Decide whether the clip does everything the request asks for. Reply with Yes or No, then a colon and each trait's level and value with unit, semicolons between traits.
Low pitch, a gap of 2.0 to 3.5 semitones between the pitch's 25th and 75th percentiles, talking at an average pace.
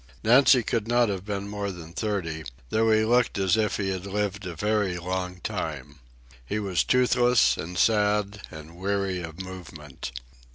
Yes: low, 100 Hz; average, 3.2 semitones; average, 165 wpm